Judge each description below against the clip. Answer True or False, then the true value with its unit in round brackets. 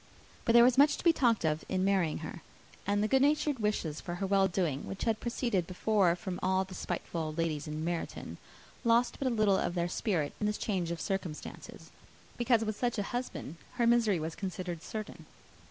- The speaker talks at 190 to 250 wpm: True (200 wpm)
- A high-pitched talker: True (195 Hz)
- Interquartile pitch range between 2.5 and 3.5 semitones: False (5.1 semitones)